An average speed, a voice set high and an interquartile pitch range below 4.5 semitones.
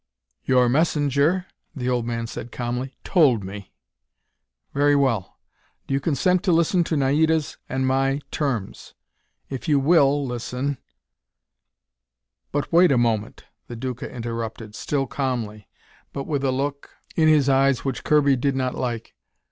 No: average, 145 wpm; low, 135 Hz; average, 3.3 semitones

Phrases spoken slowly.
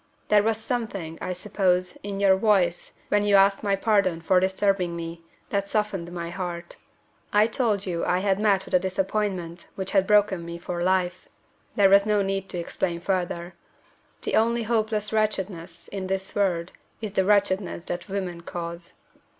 No: average, 170 wpm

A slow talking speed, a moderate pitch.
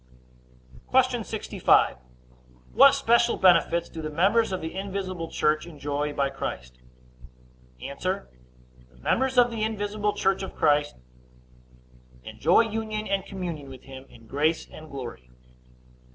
Yes: slow, 125 wpm; medium, 165 Hz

